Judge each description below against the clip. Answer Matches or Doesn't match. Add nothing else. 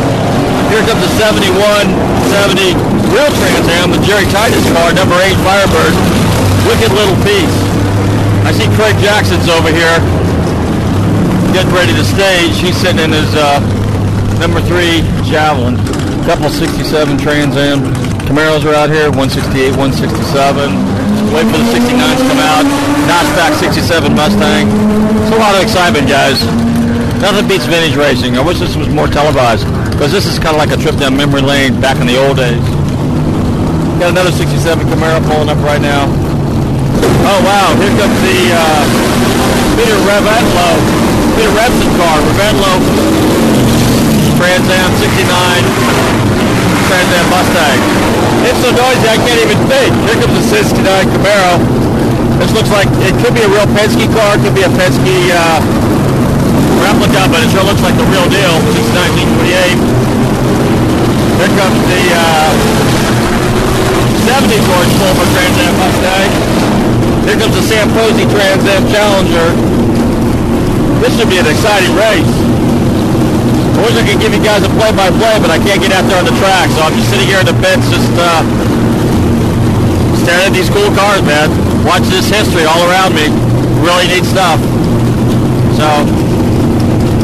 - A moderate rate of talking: Matches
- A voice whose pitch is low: Matches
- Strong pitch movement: Matches